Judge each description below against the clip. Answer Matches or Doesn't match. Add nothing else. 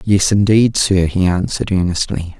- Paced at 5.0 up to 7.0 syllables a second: Doesn't match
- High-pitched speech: Doesn't match